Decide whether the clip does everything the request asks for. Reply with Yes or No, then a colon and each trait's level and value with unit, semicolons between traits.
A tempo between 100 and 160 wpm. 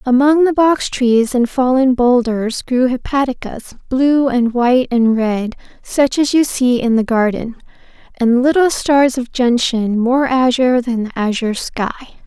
Yes: average, 155 wpm